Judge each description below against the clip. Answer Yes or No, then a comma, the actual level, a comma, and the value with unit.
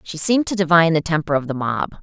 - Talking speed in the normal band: No, fast, 265 wpm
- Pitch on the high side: No, medium, 165 Hz